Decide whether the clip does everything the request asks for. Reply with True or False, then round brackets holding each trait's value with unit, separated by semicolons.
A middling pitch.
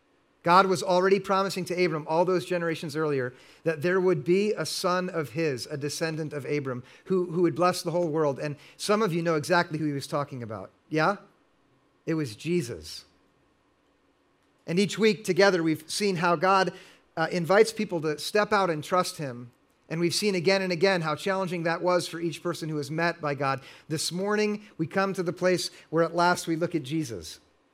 True (170 Hz)